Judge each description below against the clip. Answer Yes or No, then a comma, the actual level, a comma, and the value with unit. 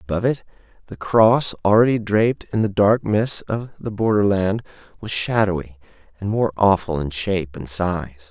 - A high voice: No, low, 100 Hz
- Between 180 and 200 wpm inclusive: No, average, 160 wpm